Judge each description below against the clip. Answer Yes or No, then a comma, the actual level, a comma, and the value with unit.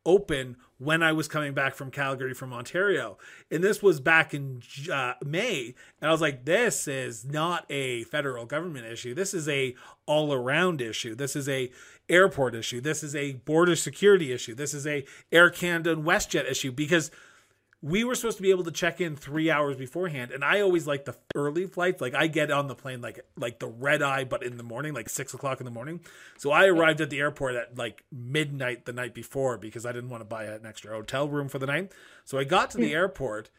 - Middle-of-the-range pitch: Yes, medium, 145 Hz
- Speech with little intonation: No, average, 4.2 semitones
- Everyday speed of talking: No, fast, 220 wpm